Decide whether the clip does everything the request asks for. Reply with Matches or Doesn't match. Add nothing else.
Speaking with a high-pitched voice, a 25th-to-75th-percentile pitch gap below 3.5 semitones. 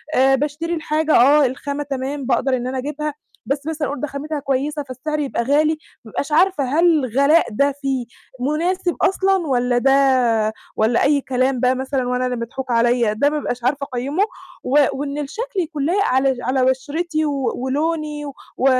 Matches